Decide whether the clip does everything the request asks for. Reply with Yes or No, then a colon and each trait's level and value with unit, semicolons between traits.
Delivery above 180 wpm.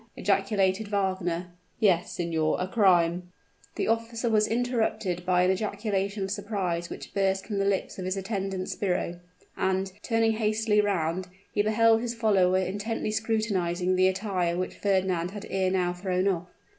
No: average, 155 wpm